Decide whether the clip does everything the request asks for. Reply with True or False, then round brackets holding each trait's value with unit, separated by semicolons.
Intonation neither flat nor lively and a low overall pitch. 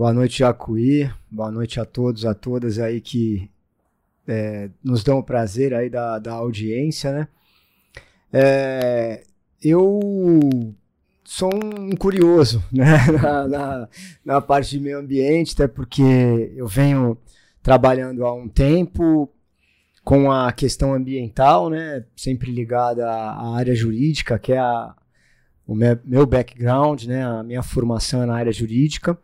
True (3.3 semitones; 125 Hz)